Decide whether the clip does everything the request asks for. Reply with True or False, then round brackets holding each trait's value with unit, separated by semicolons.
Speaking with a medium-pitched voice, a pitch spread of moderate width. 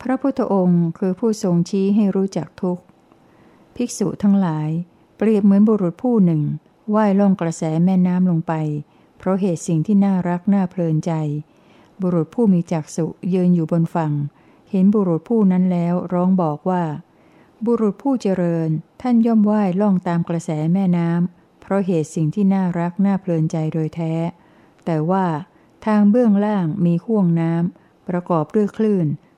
True (180 Hz; 3.3 semitones)